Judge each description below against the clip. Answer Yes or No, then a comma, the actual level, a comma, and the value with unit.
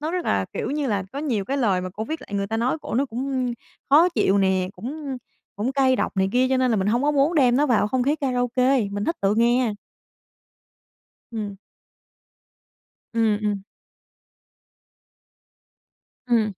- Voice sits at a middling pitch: No, high, 245 Hz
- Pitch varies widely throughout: No, average, 4.7 semitones